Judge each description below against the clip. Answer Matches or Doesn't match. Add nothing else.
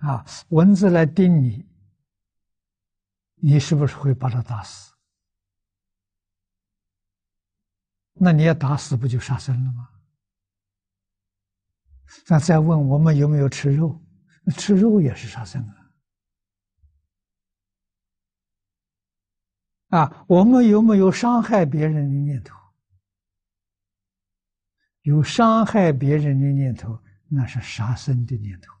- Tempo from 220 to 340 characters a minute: Doesn't match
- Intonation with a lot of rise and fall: Matches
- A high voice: Doesn't match